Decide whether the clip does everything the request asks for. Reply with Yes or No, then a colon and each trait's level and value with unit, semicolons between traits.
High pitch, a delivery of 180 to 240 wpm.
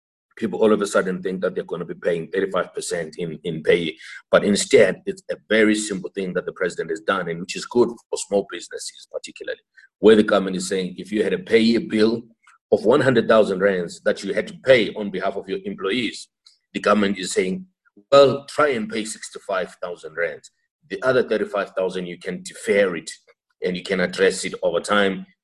Yes: high, 245 Hz; average, 200 wpm